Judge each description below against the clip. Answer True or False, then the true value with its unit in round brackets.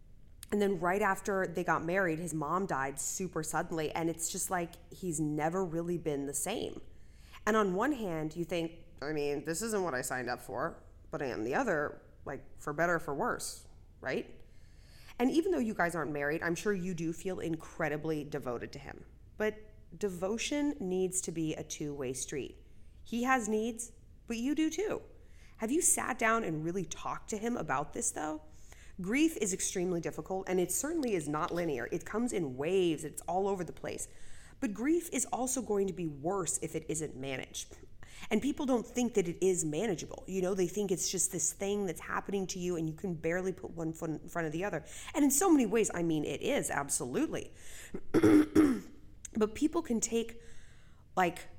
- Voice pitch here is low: False (185 Hz)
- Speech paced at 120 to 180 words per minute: False (200 wpm)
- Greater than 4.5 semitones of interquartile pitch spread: True (5.3 semitones)